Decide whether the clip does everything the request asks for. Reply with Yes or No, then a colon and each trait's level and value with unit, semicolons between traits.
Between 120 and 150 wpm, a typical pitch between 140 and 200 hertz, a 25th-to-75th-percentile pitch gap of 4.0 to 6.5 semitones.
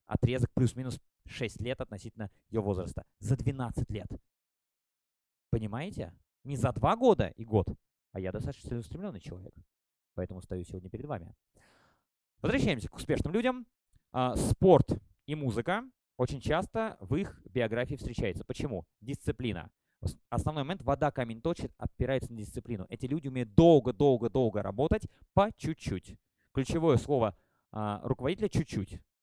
No: average, 130 wpm; low, 125 Hz; average, 5.3 semitones